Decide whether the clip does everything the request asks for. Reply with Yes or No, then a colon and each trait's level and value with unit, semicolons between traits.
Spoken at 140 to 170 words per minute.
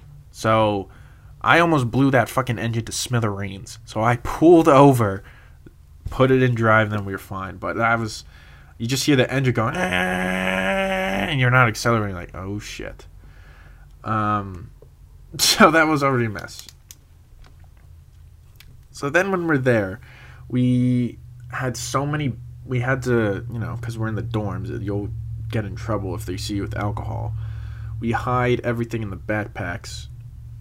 Yes: average, 160 wpm